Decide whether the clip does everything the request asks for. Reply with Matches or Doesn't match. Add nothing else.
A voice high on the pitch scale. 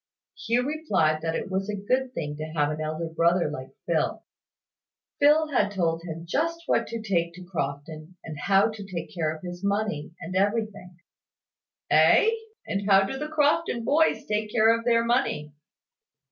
Matches